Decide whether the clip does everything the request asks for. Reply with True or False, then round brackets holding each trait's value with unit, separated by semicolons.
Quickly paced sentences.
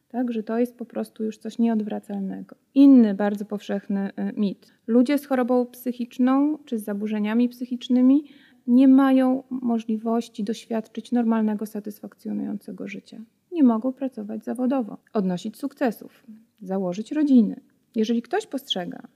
False (120 wpm)